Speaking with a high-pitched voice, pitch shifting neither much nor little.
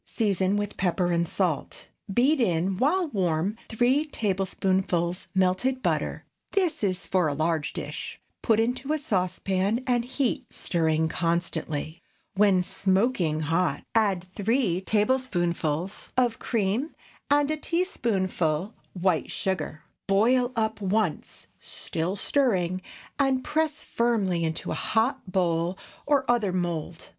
No: high, 195 Hz; wide, 5.7 semitones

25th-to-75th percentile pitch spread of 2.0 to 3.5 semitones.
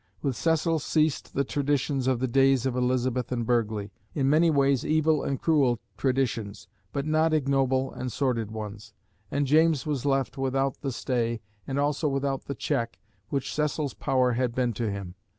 Yes: average, 2.8 semitones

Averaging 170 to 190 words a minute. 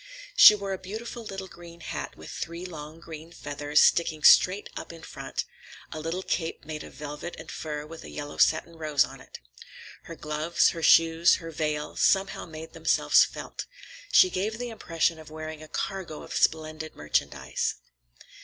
Yes: average, 175 wpm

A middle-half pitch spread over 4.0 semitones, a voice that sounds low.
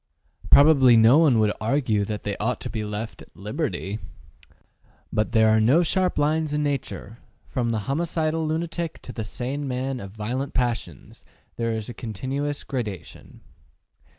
Yes: average, 5.0 semitones; low, 125 Hz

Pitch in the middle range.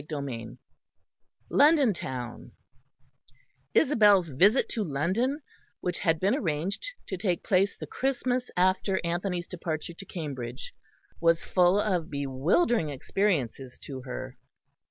Yes: medium, 175 Hz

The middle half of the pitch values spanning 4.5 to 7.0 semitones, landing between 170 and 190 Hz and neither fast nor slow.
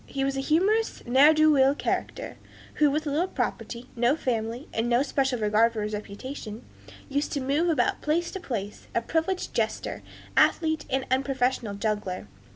No: average, 4.8 semitones; very high, 270 Hz; average, 175 wpm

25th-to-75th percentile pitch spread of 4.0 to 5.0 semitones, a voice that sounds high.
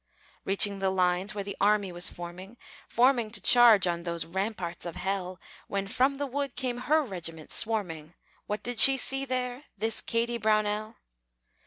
Yes: average, 4.7 semitones; high, 210 Hz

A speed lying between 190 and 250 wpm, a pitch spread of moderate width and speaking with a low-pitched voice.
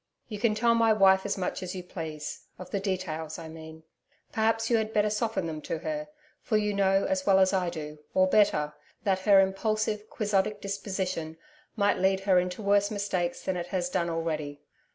No: average, 195 wpm; average, 3.3 semitones; high, 190 Hz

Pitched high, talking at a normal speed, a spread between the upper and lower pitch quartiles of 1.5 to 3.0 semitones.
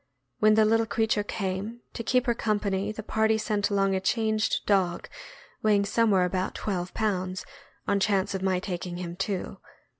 Yes: high, 200 Hz; average, 170 wpm; narrow, 2.5 semitones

